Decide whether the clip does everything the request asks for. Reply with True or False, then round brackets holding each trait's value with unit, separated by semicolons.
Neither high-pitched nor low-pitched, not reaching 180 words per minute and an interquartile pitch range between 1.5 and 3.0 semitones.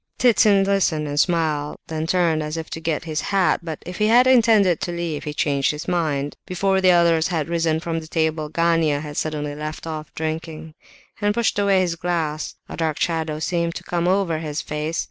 False (165 Hz; 205 wpm; 2.5 semitones)